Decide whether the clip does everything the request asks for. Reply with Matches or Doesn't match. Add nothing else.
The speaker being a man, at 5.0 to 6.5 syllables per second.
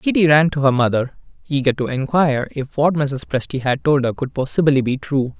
Matches